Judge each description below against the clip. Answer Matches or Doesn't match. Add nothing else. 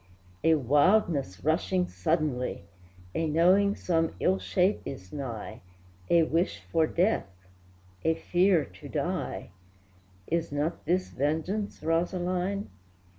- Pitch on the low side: Doesn't match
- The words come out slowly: Matches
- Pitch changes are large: Doesn't match